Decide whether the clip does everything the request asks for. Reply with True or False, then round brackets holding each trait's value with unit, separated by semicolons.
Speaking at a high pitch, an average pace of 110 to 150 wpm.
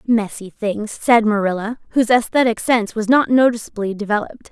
True (220 Hz; 145 wpm)